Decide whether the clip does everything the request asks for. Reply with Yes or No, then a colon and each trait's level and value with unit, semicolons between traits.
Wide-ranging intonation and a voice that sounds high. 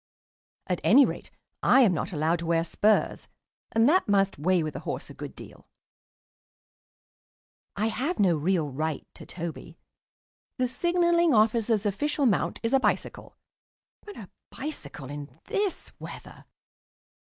Yes: wide, 8.2 semitones; high, 205 Hz